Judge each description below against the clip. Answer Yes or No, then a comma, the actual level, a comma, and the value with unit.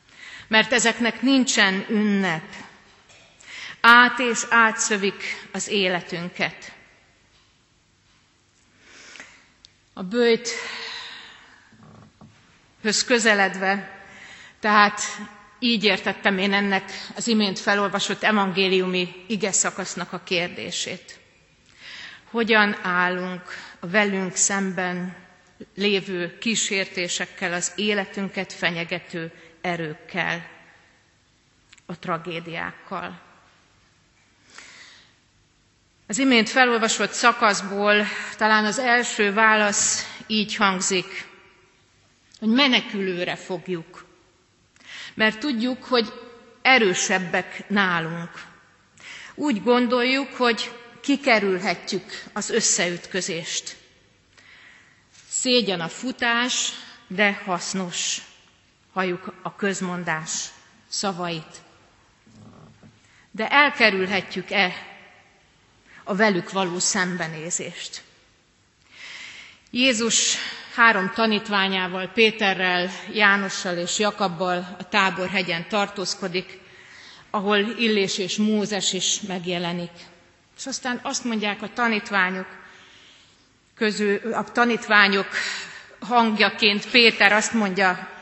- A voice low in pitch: No, high, 200 Hz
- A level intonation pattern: No, average, 3.3 semitones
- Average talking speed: No, slow, 70 wpm